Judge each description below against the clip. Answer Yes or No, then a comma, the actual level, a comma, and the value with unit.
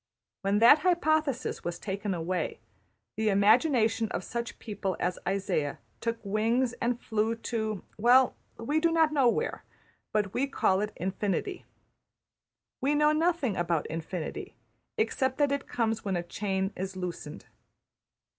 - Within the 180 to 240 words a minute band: No, average, 140 wpm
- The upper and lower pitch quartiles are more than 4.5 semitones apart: Yes, wide, 5.5 semitones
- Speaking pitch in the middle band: No, high, 220 Hz